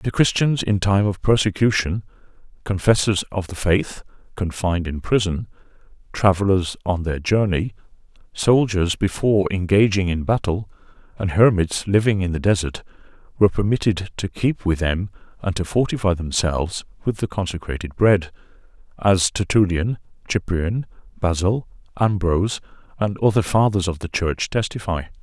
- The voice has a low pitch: Yes, very low, 95 Hz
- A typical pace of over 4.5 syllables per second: Yes, 5.0 syllables/s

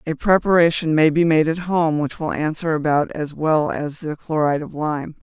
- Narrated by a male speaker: No, female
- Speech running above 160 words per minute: Yes, fast, 205 wpm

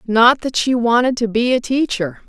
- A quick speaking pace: Yes, fast, 210 wpm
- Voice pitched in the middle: No, high, 235 Hz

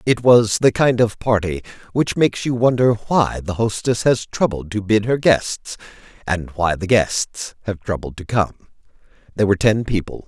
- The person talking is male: Yes, male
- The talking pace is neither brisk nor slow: Yes, average, 180 wpm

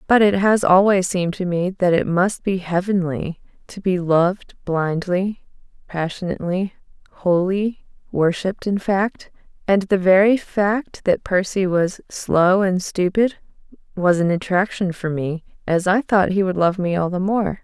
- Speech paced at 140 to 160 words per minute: Yes, average, 155 wpm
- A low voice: No, medium, 185 Hz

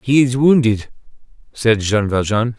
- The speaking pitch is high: No, low, 115 Hz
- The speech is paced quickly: No, average, 140 wpm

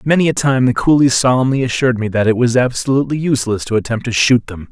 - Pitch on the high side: No, low, 125 Hz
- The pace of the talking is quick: Yes, fast, 230 wpm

